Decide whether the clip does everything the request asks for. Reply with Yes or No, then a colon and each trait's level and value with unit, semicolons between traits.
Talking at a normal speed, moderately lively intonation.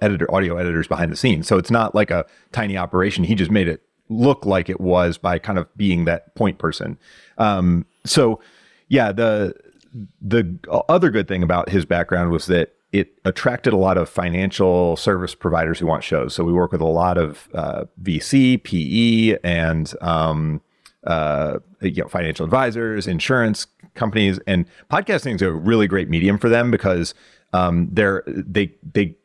Yes: average, 175 wpm; average, 3.6 semitones